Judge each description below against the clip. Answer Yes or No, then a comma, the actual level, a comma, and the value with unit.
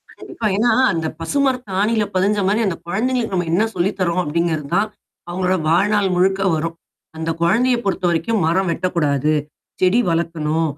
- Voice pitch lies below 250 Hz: Yes, medium, 185 Hz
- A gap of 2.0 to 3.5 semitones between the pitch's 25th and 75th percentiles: No, average, 4.2 semitones